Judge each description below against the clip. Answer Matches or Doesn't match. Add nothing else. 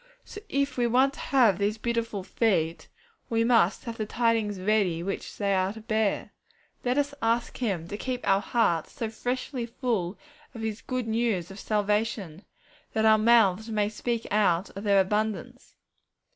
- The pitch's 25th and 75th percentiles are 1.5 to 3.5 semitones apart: Matches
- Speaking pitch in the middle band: Doesn't match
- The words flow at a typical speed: Matches